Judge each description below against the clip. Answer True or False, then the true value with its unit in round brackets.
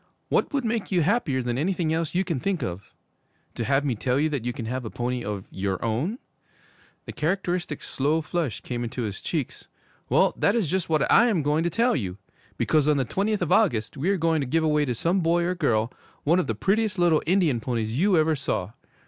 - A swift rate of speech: True (225 wpm)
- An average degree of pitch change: False (6.5 semitones)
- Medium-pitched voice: True (155 Hz)